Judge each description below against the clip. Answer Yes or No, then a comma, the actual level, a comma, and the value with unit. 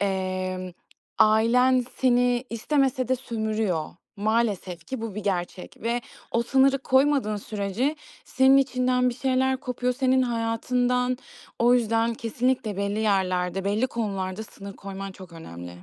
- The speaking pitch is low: No, high, 230 Hz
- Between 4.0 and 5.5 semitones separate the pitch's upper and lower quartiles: Yes, average, 4.3 semitones